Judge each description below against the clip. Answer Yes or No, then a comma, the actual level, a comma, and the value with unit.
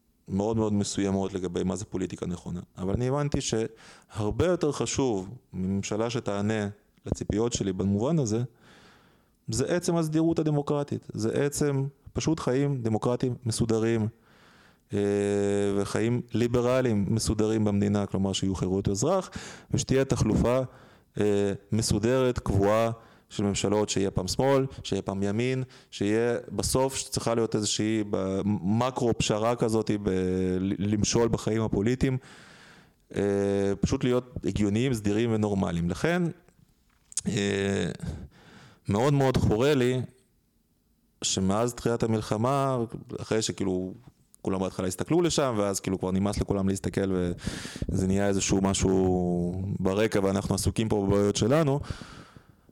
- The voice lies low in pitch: Yes, low, 110 Hz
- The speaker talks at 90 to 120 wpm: Yes, average, 110 wpm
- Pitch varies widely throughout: No, average, 4.3 semitones